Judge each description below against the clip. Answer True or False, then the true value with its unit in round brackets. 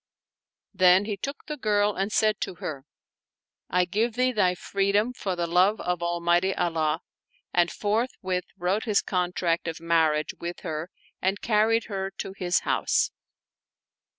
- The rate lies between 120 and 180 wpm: True (155 wpm)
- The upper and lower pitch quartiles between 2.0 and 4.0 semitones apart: True (3.3 semitones)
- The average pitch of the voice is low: False (185 Hz)